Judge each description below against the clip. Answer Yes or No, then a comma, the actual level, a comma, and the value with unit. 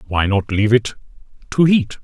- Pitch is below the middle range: Yes, low, 115 Hz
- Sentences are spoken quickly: No, average, 175 wpm